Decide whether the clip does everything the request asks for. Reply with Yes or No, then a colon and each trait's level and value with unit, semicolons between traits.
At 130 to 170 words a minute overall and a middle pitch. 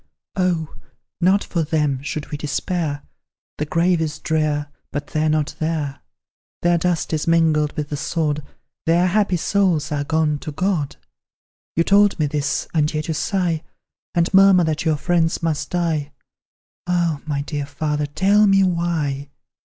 Yes: average, 160 wpm; medium, 160 Hz